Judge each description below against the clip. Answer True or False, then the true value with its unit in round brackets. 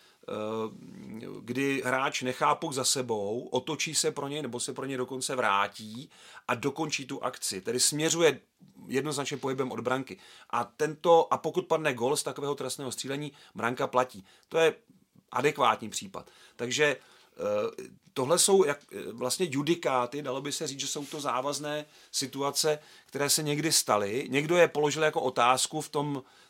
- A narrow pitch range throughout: False (3.2 semitones)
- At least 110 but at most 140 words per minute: False (155 wpm)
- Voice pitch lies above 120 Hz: True (140 Hz)